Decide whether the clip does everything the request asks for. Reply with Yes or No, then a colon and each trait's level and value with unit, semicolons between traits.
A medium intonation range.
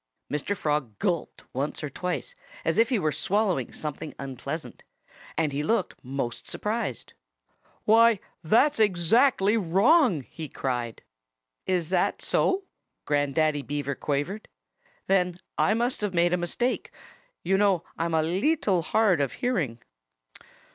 No: wide, 6.3 semitones